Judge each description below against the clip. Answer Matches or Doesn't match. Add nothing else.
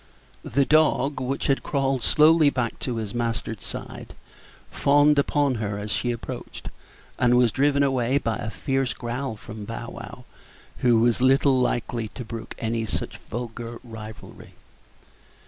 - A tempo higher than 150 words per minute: Doesn't match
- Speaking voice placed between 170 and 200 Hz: Doesn't match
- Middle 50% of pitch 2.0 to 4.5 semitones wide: Matches